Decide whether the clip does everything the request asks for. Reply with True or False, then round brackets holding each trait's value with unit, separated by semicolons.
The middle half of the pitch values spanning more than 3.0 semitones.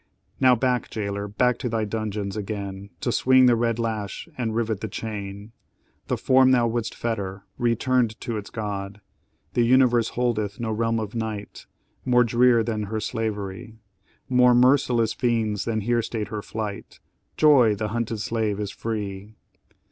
False (2.4 semitones)